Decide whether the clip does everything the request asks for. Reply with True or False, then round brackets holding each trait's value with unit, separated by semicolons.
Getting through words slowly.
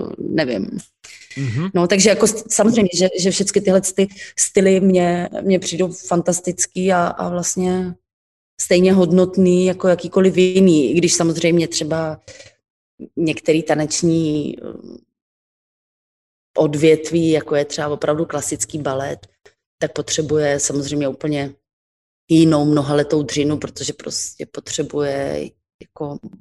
True (105 wpm)